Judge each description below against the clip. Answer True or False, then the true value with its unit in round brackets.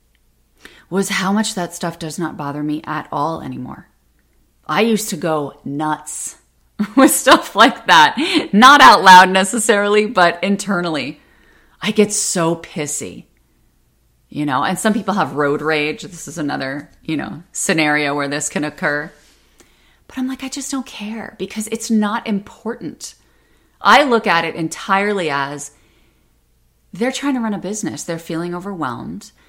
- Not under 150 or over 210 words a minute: True (155 wpm)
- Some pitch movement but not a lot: False (6.0 semitones)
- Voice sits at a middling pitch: True (170 Hz)